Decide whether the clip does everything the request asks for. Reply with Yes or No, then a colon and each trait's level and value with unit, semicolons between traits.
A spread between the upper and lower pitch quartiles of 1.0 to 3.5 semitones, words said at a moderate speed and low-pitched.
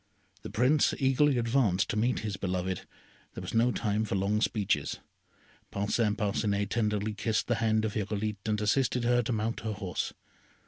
Yes: narrow, 2.5 semitones; average, 170 wpm; low, 110 Hz